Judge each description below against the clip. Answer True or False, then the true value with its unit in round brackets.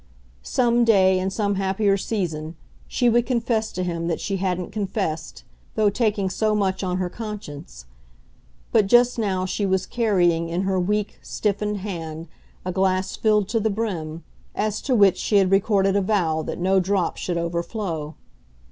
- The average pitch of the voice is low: False (195 Hz)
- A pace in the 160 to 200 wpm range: True (165 wpm)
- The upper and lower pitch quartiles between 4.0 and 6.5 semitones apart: False (3.0 semitones)